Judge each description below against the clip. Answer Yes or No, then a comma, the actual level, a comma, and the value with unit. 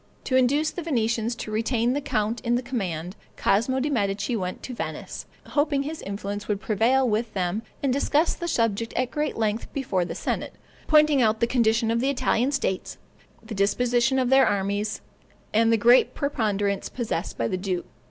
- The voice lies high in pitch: Yes, high, 230 Hz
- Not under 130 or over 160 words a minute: No, average, 180 wpm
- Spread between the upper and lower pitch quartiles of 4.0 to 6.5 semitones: Yes, average, 4.3 semitones